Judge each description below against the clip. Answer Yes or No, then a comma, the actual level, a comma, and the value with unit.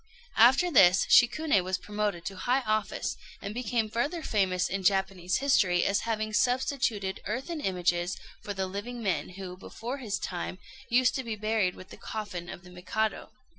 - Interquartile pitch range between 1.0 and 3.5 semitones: No, average, 4.4 semitones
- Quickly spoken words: No, average, 170 wpm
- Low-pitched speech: No, high, 210 Hz